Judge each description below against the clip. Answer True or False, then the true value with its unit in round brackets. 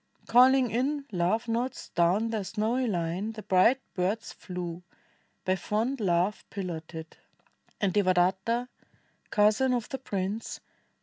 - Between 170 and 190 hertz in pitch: False (210 Hz)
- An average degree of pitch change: True (4.5 semitones)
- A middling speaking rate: False (120 wpm)